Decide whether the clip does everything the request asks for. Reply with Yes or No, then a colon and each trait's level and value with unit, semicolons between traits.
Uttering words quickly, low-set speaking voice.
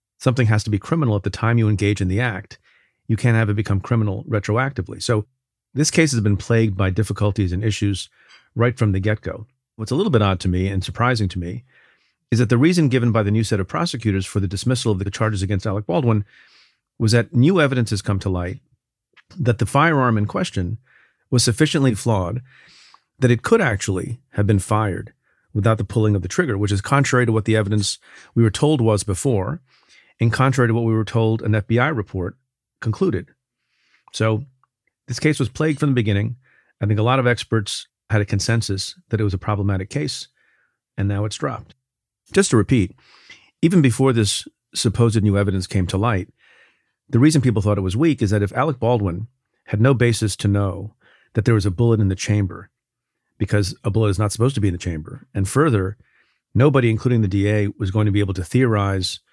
Yes: fast, 210 wpm; low, 110 Hz